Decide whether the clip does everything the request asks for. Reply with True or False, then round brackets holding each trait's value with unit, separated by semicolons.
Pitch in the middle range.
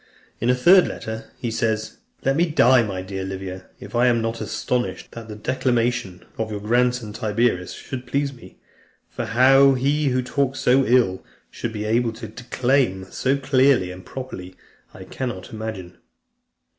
False (120 Hz)